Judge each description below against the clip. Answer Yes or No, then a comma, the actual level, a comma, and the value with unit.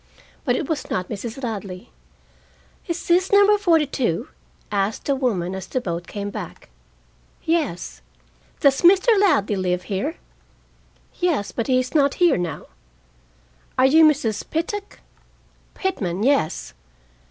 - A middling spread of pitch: No, wide, 8.7 semitones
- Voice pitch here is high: Yes, very high, 255 Hz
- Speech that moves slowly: Yes, slow, 130 wpm